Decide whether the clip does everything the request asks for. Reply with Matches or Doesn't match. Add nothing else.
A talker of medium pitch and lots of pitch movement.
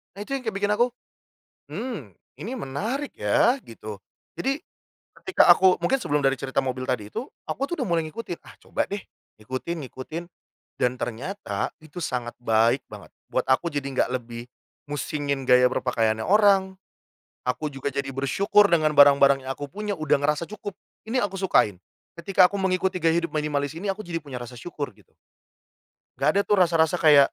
Matches